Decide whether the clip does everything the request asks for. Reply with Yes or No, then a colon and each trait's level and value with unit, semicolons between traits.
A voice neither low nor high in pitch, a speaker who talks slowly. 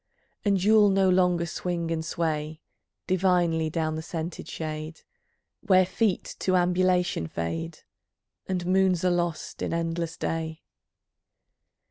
Yes: medium, 175 Hz; slow, 120 wpm